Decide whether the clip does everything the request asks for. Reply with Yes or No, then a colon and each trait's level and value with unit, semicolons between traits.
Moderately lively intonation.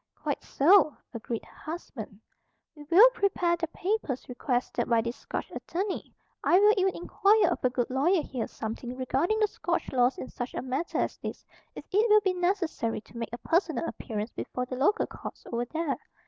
No: wide, 7.2 semitones